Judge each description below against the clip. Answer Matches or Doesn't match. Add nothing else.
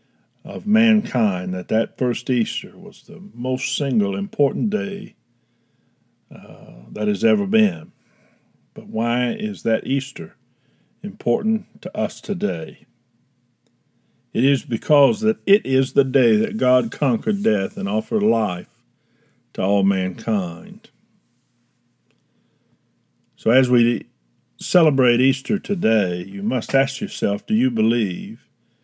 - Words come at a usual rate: Doesn't match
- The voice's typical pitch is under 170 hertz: Matches